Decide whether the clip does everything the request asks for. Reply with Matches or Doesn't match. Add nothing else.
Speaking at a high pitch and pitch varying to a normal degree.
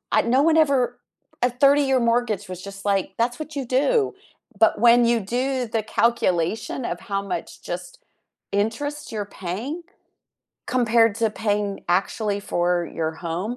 Matches